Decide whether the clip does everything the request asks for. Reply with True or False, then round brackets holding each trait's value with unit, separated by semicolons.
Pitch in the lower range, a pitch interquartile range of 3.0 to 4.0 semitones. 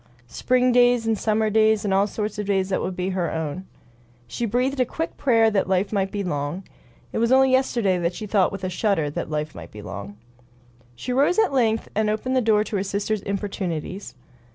False (205 Hz; 3.7 semitones)